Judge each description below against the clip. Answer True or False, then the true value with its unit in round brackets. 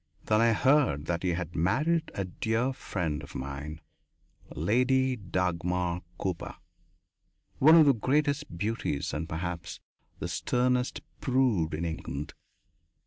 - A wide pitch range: True (7.5 semitones)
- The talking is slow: True (125 wpm)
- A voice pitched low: True (95 Hz)